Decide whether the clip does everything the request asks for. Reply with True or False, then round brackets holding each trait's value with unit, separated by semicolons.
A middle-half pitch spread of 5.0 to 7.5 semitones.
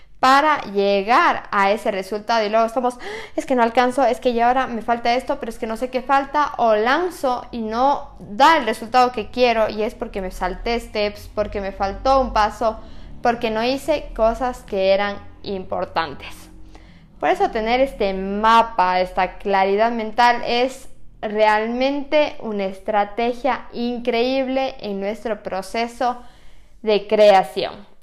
False (3.5 semitones)